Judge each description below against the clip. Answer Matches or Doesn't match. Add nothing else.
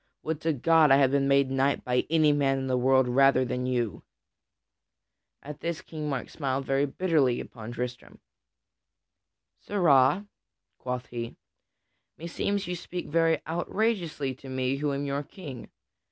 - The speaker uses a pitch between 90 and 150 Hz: Matches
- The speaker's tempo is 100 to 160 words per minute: Matches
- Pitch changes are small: Doesn't match